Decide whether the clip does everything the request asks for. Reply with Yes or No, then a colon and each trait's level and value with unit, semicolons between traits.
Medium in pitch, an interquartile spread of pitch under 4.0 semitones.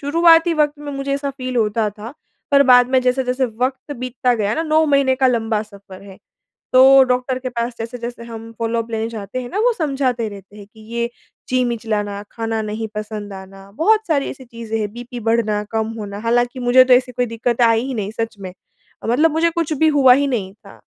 No: high, 240 Hz; average, 3.2 semitones